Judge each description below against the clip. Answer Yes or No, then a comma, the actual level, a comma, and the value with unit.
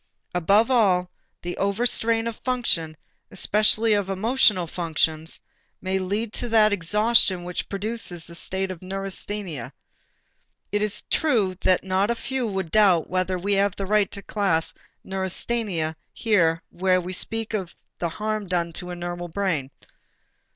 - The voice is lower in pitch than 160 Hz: No, high, 195 Hz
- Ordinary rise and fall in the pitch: Yes, average, 3.3 semitones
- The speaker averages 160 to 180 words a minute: No, average, 145 wpm